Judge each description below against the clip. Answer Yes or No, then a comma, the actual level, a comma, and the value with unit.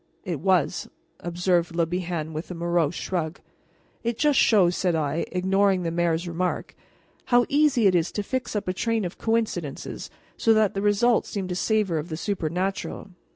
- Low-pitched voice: No, medium, 185 Hz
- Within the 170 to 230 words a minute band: Yes, average, 175 wpm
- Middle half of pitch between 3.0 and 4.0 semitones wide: Yes, average, 3.6 semitones